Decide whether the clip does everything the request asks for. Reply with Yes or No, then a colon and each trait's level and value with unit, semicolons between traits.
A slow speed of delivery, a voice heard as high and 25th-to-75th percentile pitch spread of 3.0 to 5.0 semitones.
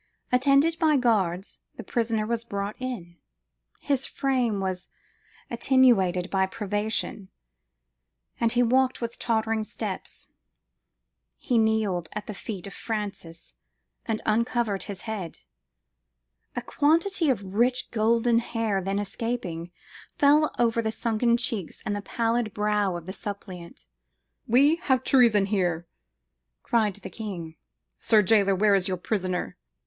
Yes: slow, 125 wpm; high, 220 Hz; average, 3.7 semitones